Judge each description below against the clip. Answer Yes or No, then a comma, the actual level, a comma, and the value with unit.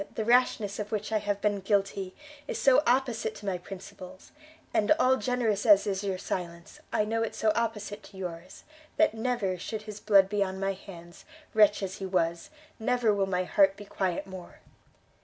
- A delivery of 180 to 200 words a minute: Yes, average, 190 wpm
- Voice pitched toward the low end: No, high, 205 Hz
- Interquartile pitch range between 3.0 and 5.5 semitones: No, narrow, 2.6 semitones